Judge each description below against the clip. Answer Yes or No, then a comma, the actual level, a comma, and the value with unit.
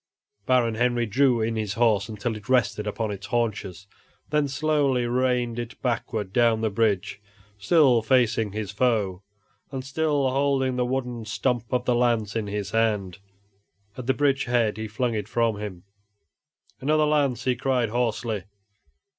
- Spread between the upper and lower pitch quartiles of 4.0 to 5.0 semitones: No, average, 3.2 semitones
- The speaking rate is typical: Yes, average, 155 wpm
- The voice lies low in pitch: Yes, low, 120 Hz